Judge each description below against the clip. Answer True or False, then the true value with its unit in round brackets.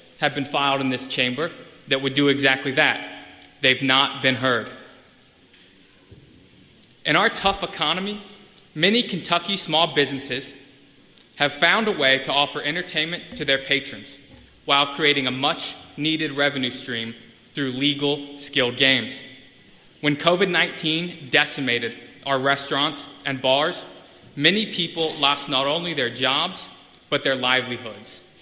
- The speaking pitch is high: False (140 Hz)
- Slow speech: True (130 wpm)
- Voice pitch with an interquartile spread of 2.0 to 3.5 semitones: True (2.9 semitones)